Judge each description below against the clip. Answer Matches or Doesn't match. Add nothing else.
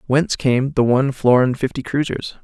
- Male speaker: Matches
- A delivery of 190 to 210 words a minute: Doesn't match